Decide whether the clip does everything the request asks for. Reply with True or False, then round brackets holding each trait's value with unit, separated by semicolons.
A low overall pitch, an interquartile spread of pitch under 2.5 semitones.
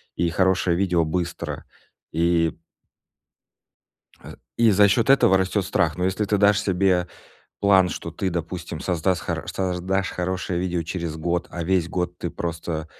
True (90 Hz; 2.0 semitones)